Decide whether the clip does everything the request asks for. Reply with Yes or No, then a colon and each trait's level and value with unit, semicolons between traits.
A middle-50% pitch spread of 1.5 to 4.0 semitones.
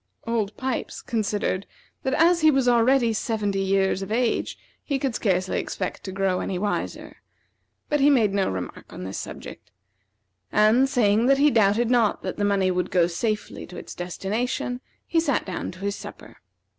No: average, 4.5 semitones